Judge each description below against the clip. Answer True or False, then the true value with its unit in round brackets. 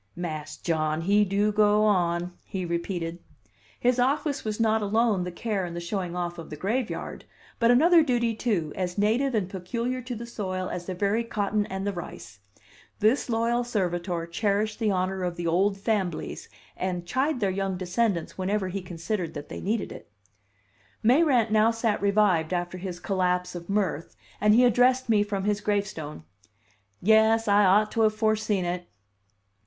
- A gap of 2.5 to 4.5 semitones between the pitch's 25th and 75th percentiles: True (3.8 semitones)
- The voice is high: True (200 Hz)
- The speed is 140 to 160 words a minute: False (170 wpm)